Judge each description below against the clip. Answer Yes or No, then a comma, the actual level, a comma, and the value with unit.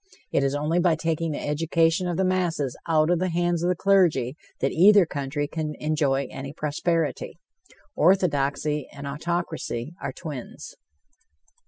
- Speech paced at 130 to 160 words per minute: Yes, average, 150 wpm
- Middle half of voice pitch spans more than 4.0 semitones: No, average, 3.2 semitones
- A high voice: No, medium, 160 Hz